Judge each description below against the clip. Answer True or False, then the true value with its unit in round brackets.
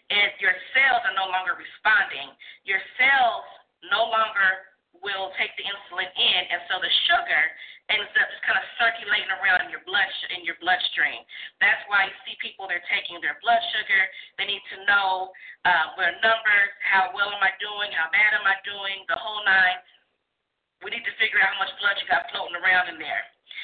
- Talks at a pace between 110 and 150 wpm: False (195 wpm)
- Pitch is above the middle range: True (200 Hz)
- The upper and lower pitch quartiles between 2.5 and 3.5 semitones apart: True (2.8 semitones)